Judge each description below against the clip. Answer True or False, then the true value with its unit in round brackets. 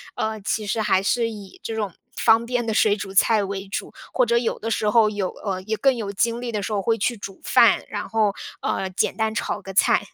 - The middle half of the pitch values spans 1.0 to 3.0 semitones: True (2.5 semitones)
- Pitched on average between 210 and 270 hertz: True (215 Hz)